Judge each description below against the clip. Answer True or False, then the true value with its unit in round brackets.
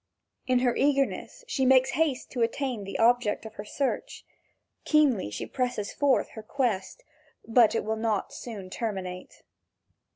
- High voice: True (240 Hz)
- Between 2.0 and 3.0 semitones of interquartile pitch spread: False (4.0 semitones)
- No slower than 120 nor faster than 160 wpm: True (155 wpm)